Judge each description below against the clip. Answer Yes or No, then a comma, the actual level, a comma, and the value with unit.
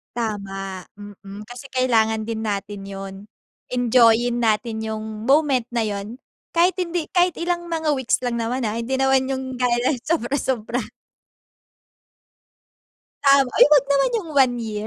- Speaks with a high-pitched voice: Yes, high, 240 Hz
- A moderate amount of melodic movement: Yes, average, 3.9 semitones